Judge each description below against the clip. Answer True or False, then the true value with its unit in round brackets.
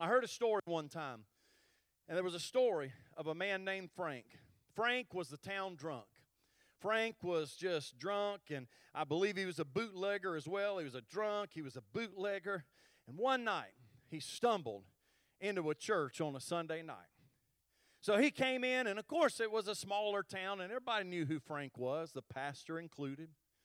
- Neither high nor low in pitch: True (180 Hz)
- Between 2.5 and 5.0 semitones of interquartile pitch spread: False (5.6 semitones)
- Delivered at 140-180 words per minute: False (190 wpm)